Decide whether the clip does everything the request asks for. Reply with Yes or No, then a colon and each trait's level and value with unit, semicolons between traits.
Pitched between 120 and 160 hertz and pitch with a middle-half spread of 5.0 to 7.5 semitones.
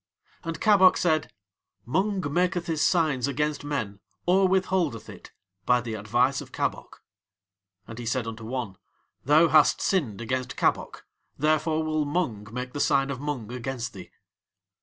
Yes: medium, 140 Hz; average, 5.3 semitones